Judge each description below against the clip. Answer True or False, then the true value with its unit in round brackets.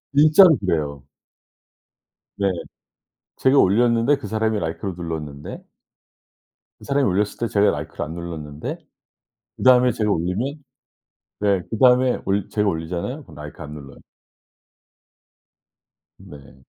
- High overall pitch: False (100 Hz)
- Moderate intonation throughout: False (7.3 semitones)